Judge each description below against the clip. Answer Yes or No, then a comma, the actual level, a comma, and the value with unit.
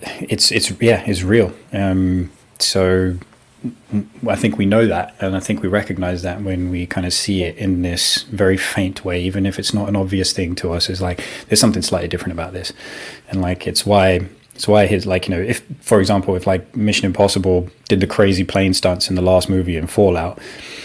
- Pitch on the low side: Yes, very low, 95 Hz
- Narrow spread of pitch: Yes, narrow, 1.9 semitones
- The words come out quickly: Yes, fast, 215 wpm